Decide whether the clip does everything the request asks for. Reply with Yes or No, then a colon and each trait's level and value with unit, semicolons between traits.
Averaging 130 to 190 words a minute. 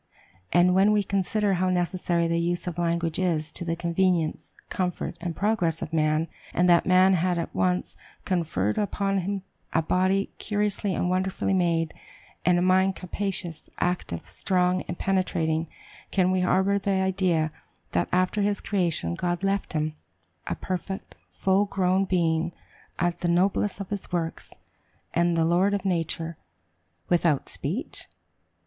Yes: average, 150 wpm